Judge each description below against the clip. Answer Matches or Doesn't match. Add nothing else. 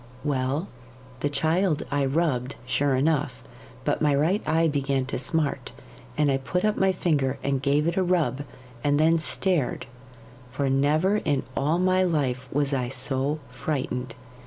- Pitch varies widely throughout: Doesn't match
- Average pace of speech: Matches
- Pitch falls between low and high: Matches